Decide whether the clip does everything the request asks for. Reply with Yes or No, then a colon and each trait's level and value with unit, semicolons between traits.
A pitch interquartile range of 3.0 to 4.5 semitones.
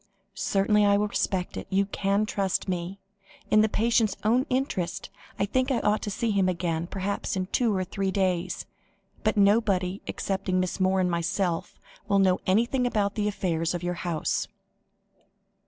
No: narrow, 2.4 semitones